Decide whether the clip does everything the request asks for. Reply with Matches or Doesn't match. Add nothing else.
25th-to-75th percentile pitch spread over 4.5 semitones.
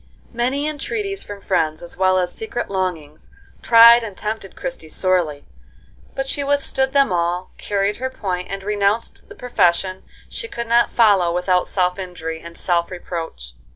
Matches